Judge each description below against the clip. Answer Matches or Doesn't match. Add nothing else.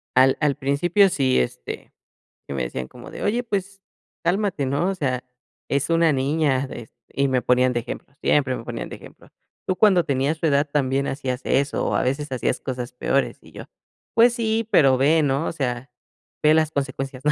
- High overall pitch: Doesn't match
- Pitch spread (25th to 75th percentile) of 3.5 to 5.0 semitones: Matches